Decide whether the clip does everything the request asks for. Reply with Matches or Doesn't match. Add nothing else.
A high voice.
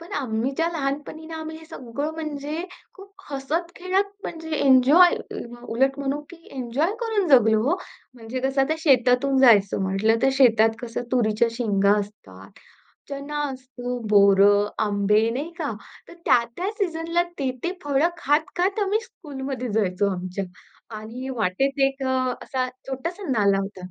Matches